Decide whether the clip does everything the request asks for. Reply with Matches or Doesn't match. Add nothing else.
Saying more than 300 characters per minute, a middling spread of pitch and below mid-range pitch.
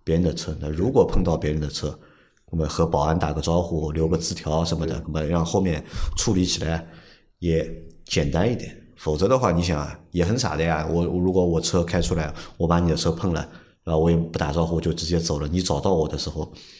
Doesn't match